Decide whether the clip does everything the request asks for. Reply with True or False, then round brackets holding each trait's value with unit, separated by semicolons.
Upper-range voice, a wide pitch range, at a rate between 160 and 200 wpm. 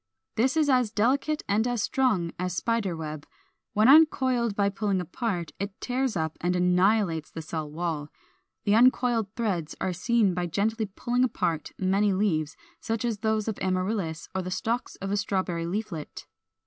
False (200 Hz; 4.7 semitones; 165 wpm)